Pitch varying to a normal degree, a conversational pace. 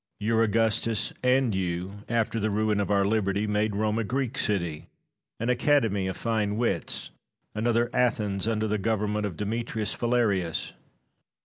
No: narrow, 2.2 semitones; average, 145 wpm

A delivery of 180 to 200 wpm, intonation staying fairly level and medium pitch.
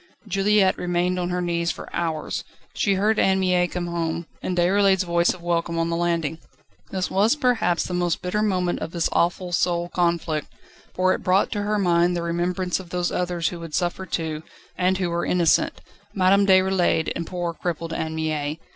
Yes: average, 190 wpm; narrow, 1.7 semitones; medium, 175 Hz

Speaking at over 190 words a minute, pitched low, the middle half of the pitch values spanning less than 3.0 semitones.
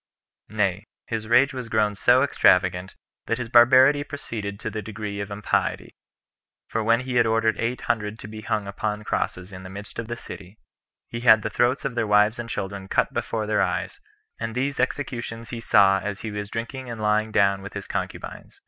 Yes: average, 200 wpm; low, 110 Hz; narrow, 2.5 semitones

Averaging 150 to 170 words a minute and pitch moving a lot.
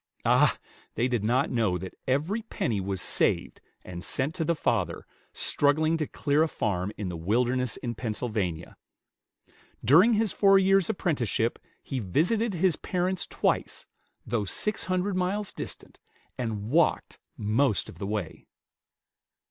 No: average, 140 wpm; wide, 9.0 semitones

